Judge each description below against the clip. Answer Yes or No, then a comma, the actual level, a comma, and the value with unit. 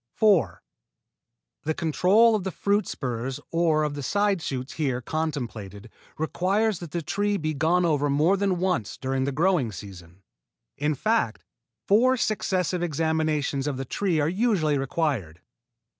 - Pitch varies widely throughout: Yes, wide, 5.8 semitones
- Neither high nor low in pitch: Yes, medium, 155 Hz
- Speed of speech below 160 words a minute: Yes, average, 145 wpm